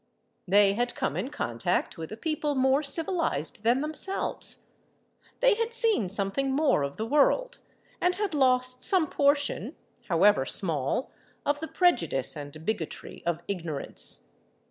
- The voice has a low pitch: No, very high, 255 Hz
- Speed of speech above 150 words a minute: No, average, 140 wpm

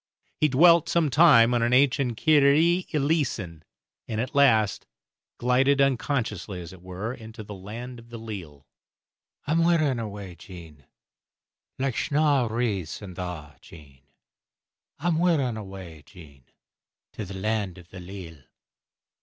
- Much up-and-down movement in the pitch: Yes, wide, 7.2 semitones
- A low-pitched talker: Yes, low, 115 Hz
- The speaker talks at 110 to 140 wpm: Yes, slow, 135 wpm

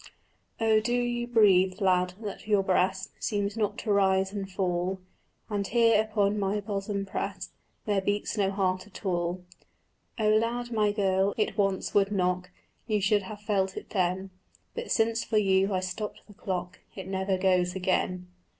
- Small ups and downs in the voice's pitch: Yes, narrow, 2.0 semitones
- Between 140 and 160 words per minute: No, average, 170 wpm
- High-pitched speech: Yes, high, 195 Hz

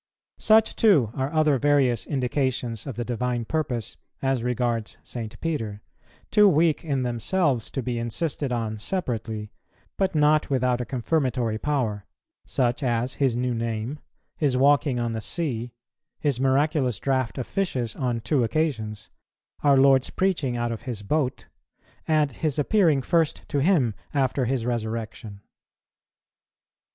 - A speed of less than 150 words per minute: Yes, average, 140 wpm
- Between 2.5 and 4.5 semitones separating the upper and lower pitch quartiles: Yes, average, 4.1 semitones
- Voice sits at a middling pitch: No, low, 130 Hz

